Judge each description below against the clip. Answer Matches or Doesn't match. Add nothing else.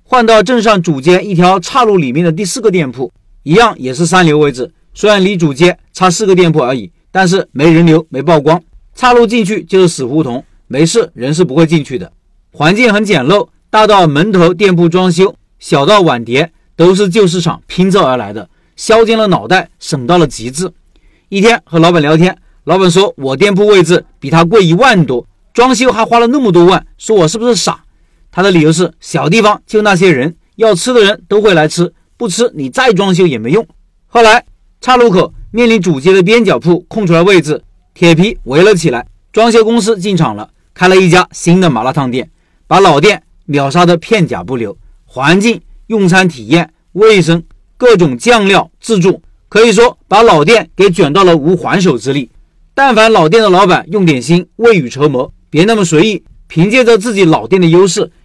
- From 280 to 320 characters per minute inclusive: Matches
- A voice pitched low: Doesn't match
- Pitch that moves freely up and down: Doesn't match